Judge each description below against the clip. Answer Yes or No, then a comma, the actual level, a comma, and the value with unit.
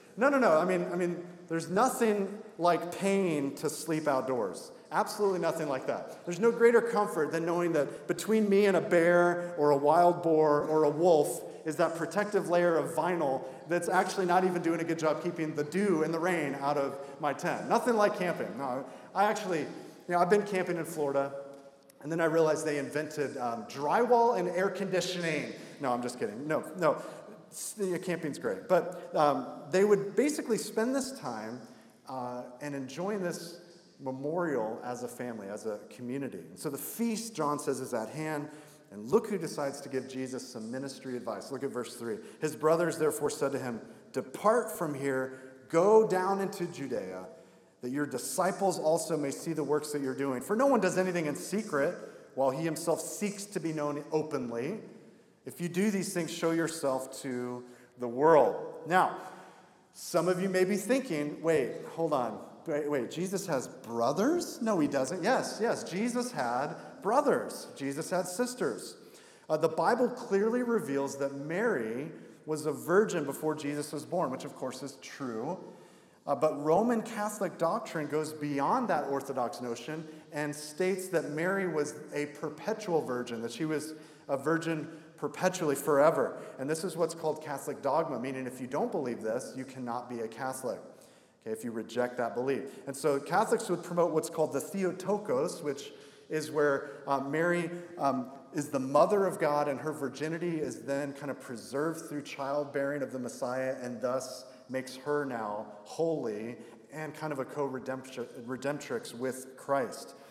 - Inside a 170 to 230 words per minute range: Yes, average, 175 wpm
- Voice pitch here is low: No, medium, 155 Hz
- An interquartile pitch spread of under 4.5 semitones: No, average, 4.8 semitones